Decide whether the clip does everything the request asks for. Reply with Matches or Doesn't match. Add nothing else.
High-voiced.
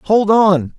Matches